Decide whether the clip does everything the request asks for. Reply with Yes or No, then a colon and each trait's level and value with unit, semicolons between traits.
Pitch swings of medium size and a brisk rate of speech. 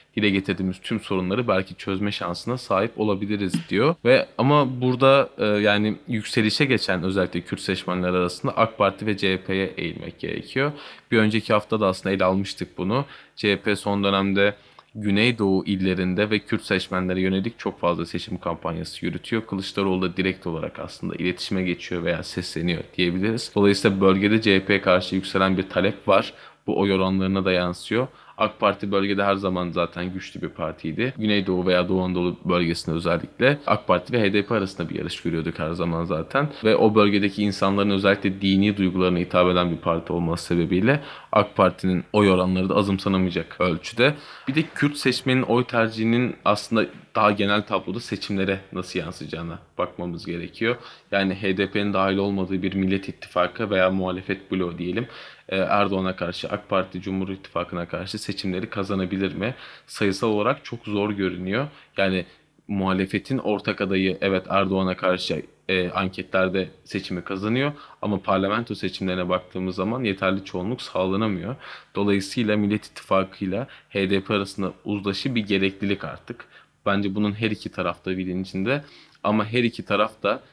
No: narrow, 2.1 semitones; fast, 150 wpm